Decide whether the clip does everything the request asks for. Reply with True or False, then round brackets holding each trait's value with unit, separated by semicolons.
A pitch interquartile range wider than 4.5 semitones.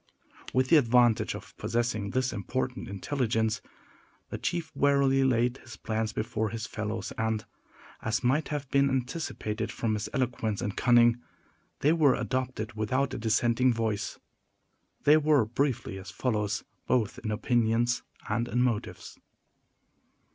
False (3.0 semitones)